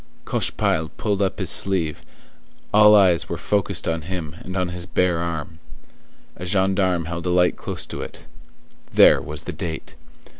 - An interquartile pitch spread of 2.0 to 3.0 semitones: Yes, narrow, 2.4 semitones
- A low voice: Yes, very low, 90 Hz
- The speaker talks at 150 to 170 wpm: Yes, average, 160 wpm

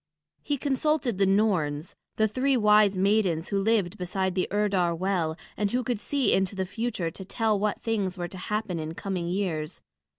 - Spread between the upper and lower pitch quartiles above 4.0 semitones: No, average, 3.3 semitones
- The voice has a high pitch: Yes, high, 195 Hz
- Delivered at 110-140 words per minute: No, average, 185 wpm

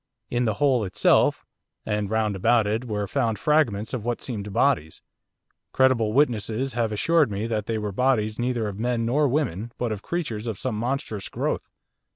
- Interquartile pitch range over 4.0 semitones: No, average, 3.0 semitones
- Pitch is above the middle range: No, low, 115 Hz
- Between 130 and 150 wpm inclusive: No, average, 180 wpm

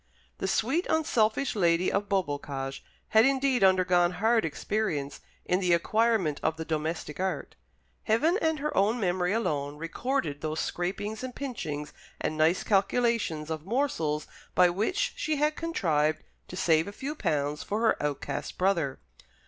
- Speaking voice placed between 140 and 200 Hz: Yes, medium, 185 Hz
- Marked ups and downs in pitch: Yes, wide, 6.8 semitones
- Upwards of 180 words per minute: No, average, 150 wpm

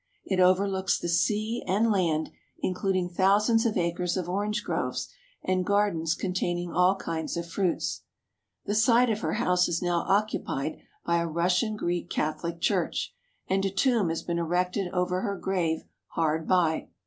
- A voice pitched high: No, medium, 180 Hz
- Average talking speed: Yes, average, 160 wpm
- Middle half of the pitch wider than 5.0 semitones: No, average, 2.8 semitones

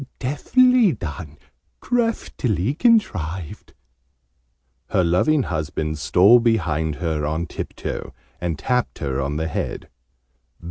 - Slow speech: Yes, slow, 100 wpm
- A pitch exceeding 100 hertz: No, very low, 90 Hz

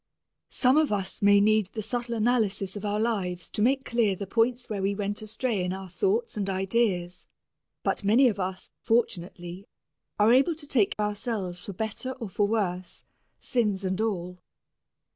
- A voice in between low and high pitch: No, high, 210 Hz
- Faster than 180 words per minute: No, average, 170 wpm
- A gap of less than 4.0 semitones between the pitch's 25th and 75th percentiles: Yes, average, 3.6 semitones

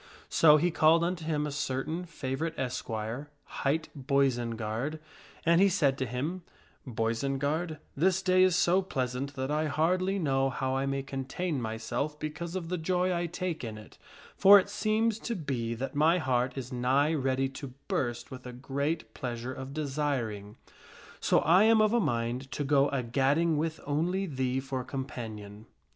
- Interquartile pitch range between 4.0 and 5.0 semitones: Yes, average, 4.5 semitones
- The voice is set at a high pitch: No, medium, 140 Hz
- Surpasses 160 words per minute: Yes, average, 170 wpm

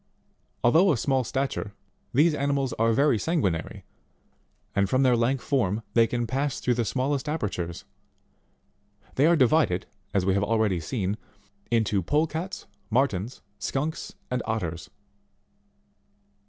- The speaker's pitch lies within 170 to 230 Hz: No, low, 125 Hz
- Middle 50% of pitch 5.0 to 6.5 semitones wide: Yes, average, 5.3 semitones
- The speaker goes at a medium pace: No, slow, 125 wpm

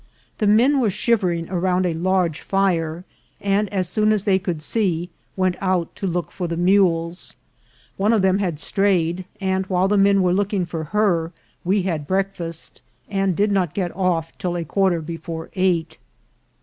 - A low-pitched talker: No, medium, 185 Hz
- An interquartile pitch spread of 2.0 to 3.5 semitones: Yes, narrow, 2.5 semitones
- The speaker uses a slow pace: No, average, 175 wpm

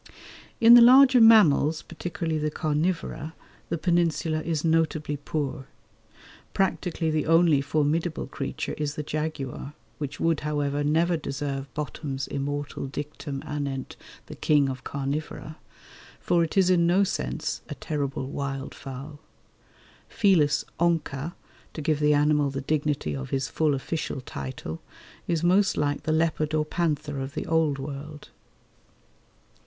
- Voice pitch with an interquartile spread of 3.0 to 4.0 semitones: No, narrow, 2.6 semitones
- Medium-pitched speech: Yes, medium, 150 Hz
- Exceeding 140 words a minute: No, slow, 135 wpm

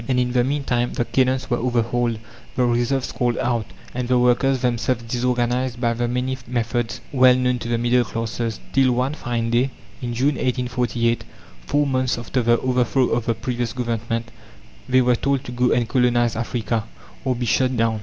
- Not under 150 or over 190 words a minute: Yes, average, 185 wpm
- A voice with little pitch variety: Yes, narrow, 1.3 semitones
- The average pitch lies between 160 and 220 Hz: No, low, 120 Hz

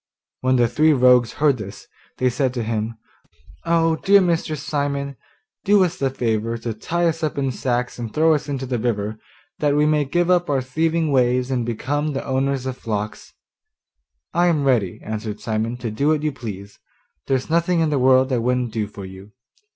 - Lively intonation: No, average, 4.7 semitones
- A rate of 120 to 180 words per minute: No, average, 195 wpm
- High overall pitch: No, low, 130 Hz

